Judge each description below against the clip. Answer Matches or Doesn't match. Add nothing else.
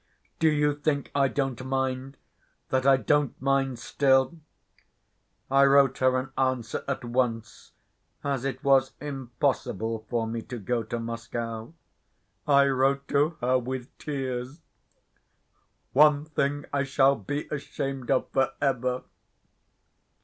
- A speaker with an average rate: Doesn't match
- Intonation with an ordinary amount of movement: Doesn't match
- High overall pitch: Doesn't match